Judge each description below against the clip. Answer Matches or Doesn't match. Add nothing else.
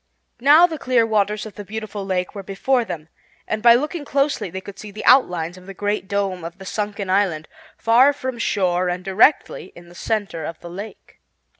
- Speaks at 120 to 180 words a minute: Doesn't match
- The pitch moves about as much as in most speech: Matches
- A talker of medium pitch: Doesn't match